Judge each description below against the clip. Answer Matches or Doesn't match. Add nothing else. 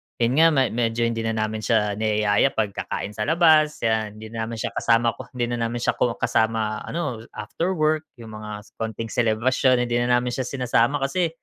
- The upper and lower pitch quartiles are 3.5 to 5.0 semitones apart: Doesn't match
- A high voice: Doesn't match